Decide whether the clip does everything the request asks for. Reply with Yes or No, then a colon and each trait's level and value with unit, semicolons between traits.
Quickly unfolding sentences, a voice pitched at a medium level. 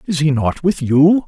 Yes: fast, 235 wpm; medium, 155 Hz